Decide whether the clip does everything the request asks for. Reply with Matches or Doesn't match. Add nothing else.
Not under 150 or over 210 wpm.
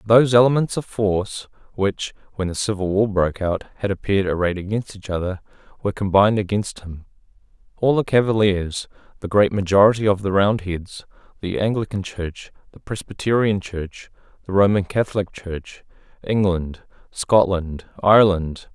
Doesn't match